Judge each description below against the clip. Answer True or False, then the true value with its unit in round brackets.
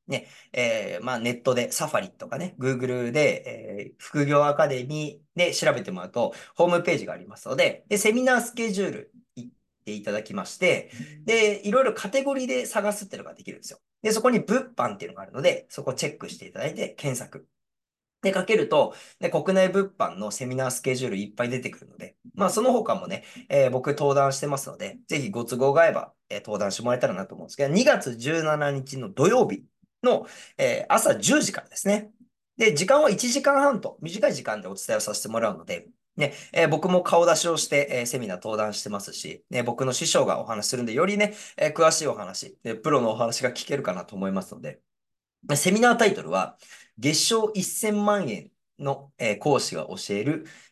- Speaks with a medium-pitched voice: True (165 Hz)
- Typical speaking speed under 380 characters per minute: False (395 characters per minute)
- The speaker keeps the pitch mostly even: False (8.7 semitones)